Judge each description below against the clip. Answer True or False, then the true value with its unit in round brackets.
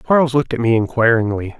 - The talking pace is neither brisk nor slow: True (190 wpm)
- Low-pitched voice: True (120 Hz)